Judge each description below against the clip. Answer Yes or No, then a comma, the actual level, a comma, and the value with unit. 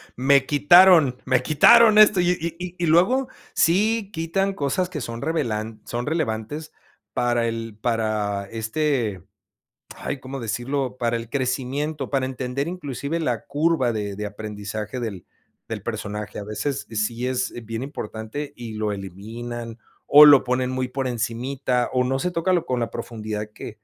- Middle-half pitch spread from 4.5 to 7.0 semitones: Yes, average, 5.1 semitones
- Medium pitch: No, low, 125 Hz